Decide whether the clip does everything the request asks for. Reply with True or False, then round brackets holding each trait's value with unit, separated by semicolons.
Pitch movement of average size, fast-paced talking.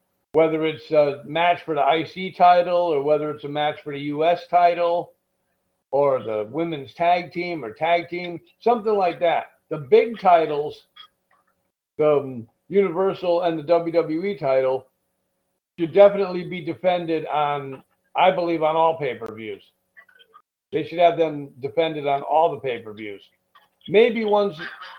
False (3.1 semitones; 150 wpm)